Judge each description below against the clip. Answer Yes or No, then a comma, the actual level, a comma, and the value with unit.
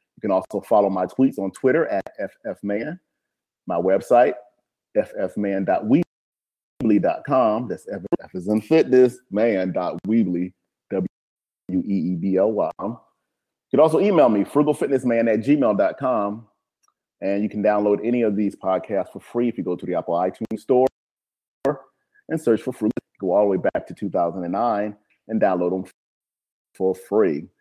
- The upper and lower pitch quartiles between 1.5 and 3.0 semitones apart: No, average, 4.1 semitones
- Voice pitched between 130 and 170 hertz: No, low, 105 Hz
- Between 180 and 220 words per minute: No, slow, 135 wpm